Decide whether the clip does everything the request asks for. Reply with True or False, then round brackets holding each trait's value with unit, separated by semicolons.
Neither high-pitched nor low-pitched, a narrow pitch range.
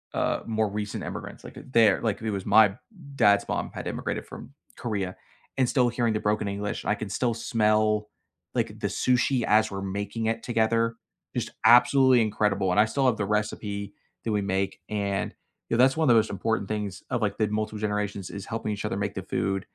False (105 Hz; 2.1 semitones)